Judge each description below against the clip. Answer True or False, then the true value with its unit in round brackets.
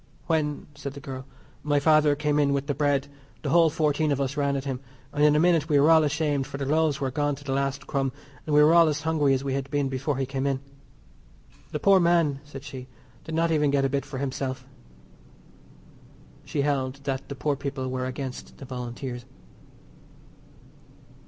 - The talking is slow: False (205 wpm)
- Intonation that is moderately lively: False (1.9 semitones)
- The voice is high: False (140 Hz)